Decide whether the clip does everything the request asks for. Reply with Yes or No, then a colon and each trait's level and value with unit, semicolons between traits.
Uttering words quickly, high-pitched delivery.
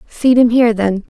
Yes: fast, 210 wpm; high, 230 Hz